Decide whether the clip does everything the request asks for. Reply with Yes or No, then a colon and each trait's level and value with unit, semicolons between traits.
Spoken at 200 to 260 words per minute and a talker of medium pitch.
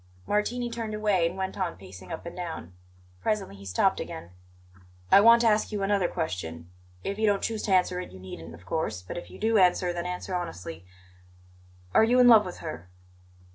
Yes: fast, 205 wpm; medium, 180 Hz